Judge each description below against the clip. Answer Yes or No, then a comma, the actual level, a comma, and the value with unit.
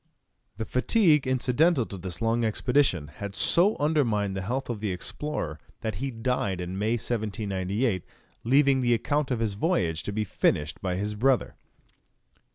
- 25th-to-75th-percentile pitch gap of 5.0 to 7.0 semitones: Yes, average, 5.3 semitones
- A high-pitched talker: No, low, 115 Hz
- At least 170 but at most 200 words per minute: No, average, 160 wpm